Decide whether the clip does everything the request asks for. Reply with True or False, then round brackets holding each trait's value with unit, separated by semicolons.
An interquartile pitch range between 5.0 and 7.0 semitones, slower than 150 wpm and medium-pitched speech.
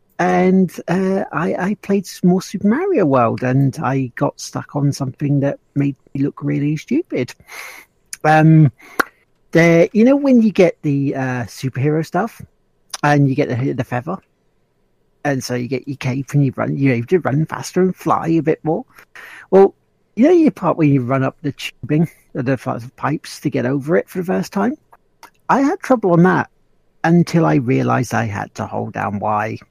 False (5.4 semitones; 190 wpm; 145 Hz)